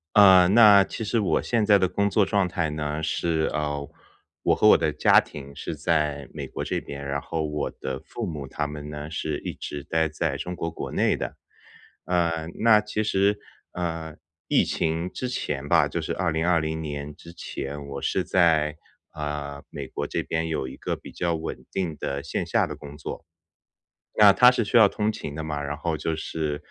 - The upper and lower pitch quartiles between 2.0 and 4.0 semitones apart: Yes, average, 3.7 semitones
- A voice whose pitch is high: No, very low, 80 Hz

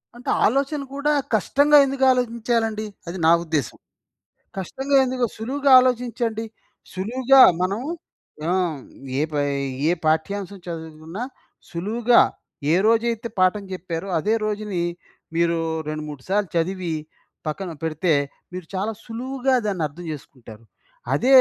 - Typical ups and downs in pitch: No, wide, 6.4 semitones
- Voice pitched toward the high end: Yes, high, 210 Hz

